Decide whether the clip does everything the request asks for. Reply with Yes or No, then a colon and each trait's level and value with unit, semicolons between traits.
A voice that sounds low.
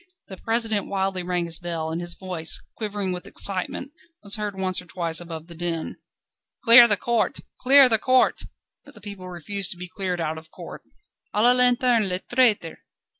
No: high, 190 Hz